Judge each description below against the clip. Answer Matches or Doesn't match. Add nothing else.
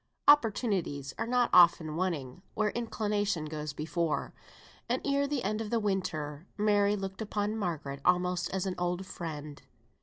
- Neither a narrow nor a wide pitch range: Matches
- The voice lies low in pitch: Doesn't match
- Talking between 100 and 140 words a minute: Doesn't match